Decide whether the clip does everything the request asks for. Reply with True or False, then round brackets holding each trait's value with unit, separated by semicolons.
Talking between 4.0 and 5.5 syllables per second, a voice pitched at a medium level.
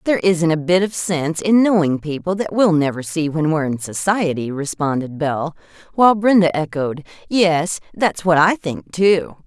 True (5.0 syllables/s; 170 Hz)